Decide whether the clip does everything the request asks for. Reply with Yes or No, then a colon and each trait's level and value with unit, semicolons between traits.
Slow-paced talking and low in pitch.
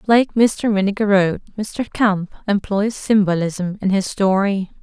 No: slow, 125 wpm; high, 200 Hz